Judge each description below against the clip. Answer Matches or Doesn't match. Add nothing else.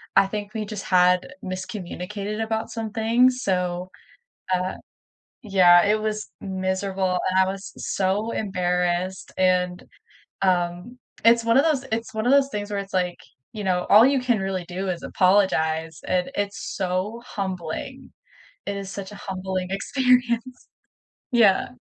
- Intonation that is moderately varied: Matches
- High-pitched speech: Matches